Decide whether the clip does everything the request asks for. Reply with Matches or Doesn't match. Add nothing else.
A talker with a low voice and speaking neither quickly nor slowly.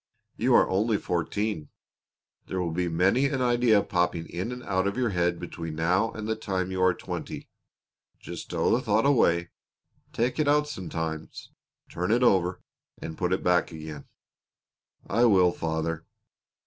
Matches